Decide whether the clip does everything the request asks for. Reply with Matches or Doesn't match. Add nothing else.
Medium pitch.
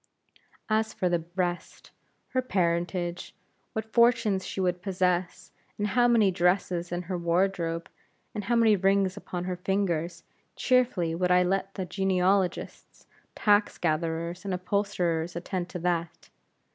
Matches